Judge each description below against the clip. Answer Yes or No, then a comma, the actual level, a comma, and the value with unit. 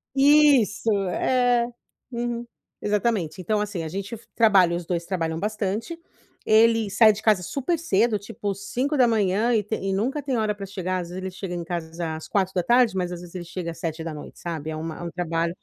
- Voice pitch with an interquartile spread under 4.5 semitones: No, average, 4.8 semitones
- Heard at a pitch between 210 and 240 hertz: No, high, 200 Hz